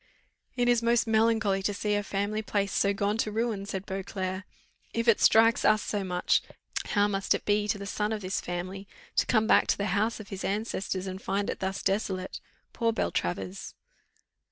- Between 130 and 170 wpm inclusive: No, average, 195 wpm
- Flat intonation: Yes, narrow, 2.2 semitones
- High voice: Yes, high, 205 Hz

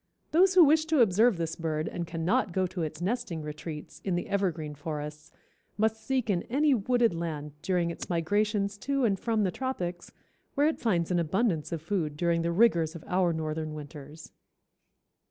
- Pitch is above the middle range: No, medium, 175 Hz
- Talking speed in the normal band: Yes, average, 180 wpm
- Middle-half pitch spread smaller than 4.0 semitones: No, wide, 5.4 semitones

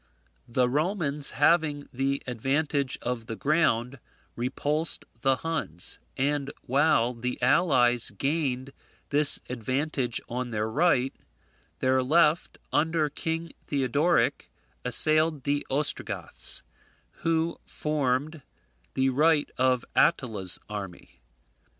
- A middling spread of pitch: Yes, average, 3.6 semitones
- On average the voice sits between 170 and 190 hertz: No, medium, 140 Hz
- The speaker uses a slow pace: Yes, slow, 100 wpm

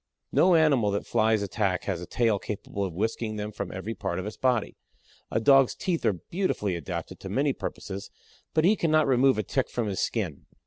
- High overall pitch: No, low, 110 Hz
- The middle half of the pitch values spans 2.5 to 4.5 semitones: No, average, 5.1 semitones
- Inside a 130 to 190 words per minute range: No, fast, 205 wpm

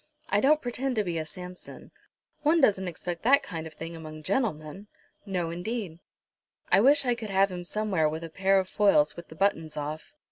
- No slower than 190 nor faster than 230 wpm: Yes, average, 200 wpm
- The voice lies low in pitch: No, medium, 185 Hz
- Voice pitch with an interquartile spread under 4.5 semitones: No, average, 5.0 semitones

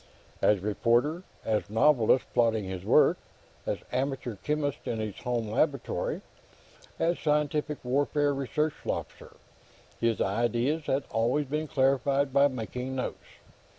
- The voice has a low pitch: Yes, low, 130 Hz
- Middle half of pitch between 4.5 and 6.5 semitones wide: No, average, 4.1 semitones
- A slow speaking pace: Yes, slow, 120 wpm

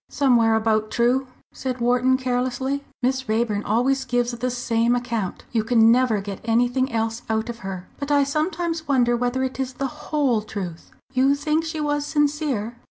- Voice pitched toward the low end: No, high, 245 Hz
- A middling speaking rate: Yes, average, 170 wpm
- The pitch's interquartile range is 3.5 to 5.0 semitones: No, average, 3.0 semitones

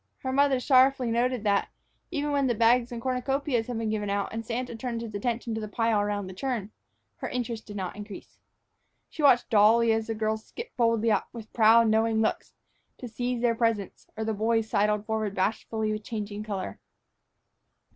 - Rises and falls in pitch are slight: Yes, narrow, 2.3 semitones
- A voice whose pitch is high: Yes, high, 225 Hz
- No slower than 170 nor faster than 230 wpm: Yes, average, 190 wpm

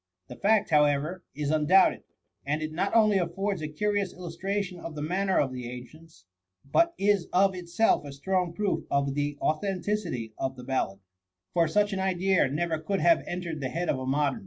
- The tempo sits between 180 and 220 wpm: Yes, average, 185 wpm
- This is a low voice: No, medium, 170 Hz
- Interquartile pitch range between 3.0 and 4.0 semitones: No, average, 4.9 semitones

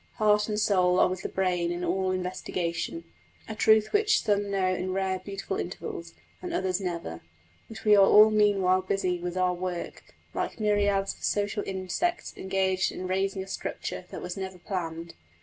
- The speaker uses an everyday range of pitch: No, narrow, 2.1 semitones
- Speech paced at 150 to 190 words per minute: Yes, average, 175 wpm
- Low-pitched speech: No, high, 190 Hz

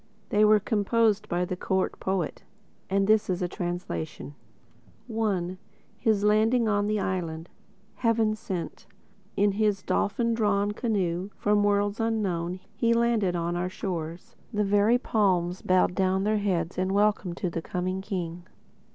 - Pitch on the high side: Yes, high, 200 Hz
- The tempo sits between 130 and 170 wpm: Yes, average, 145 wpm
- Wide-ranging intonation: No, average, 2.9 semitones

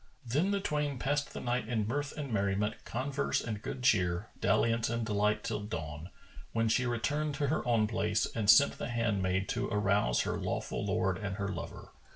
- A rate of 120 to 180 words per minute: No, average, 190 wpm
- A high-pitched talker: No, low, 115 Hz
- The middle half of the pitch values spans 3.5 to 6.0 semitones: Yes, average, 4.5 semitones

